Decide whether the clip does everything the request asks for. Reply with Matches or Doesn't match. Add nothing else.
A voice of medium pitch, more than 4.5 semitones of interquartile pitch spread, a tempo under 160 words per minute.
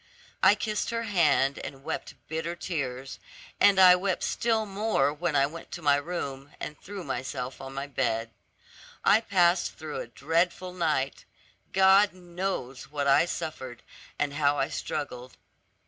Matches